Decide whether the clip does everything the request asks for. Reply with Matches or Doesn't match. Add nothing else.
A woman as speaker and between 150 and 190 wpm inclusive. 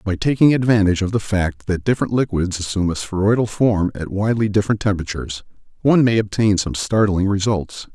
Doesn't match